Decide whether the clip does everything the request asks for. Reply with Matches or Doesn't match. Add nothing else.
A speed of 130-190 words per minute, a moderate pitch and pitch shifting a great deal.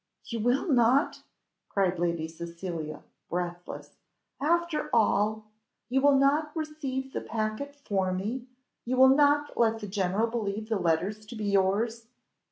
Doesn't match